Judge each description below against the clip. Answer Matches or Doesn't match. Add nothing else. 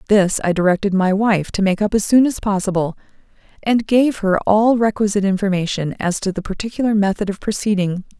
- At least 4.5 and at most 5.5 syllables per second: Doesn't match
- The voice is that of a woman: Matches